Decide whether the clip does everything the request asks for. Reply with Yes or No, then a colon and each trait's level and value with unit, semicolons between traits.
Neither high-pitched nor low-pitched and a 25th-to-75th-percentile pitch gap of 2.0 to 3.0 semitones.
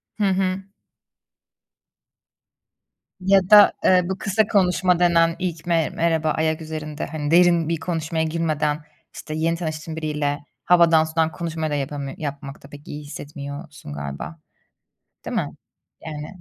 Yes: medium, 160 Hz; narrow, 2.4 semitones